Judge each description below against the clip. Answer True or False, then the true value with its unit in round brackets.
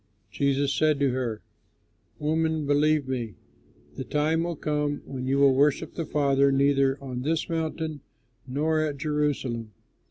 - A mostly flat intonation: True (2.3 semitones)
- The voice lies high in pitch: False (145 Hz)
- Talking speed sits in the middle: True (145 wpm)